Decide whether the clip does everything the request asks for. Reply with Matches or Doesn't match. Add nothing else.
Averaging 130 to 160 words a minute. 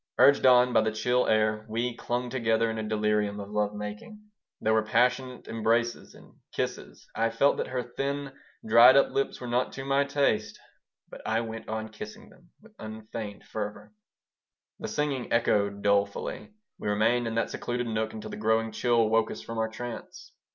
Doesn't match